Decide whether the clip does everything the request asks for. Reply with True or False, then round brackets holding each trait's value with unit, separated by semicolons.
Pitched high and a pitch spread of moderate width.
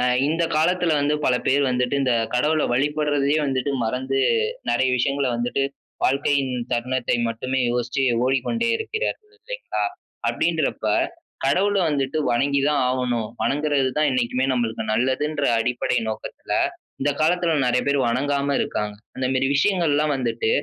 False (140 Hz; 3.1 semitones)